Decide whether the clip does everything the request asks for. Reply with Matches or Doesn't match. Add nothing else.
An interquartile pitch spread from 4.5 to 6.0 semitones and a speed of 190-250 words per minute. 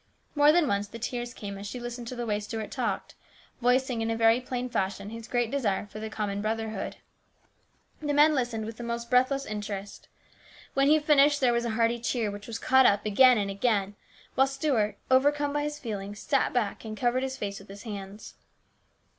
Doesn't match